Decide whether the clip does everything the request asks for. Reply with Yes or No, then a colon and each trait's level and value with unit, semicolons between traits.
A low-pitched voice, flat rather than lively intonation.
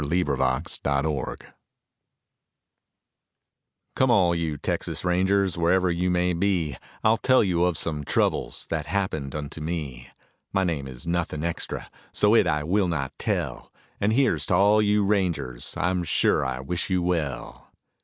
No: very low, 85 Hz; average, 4.2 semitones